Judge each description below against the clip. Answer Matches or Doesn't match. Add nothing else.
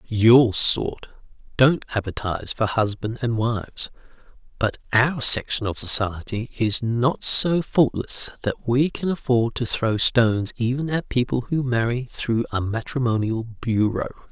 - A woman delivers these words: Doesn't match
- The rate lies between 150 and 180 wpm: Doesn't match